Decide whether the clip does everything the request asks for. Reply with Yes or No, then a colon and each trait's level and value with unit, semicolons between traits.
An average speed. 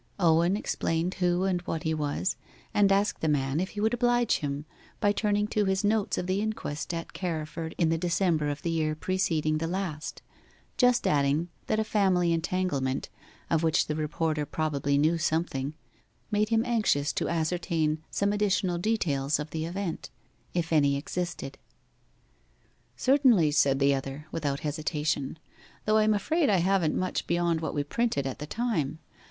Yes: average, 170 wpm